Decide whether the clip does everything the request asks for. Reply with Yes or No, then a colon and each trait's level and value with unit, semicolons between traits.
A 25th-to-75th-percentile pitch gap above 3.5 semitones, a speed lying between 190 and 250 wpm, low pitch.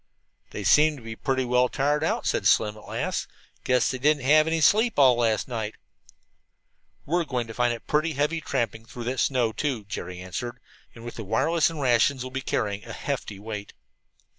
Yes: average, 4.6 semitones; average, 200 wpm; low, 125 Hz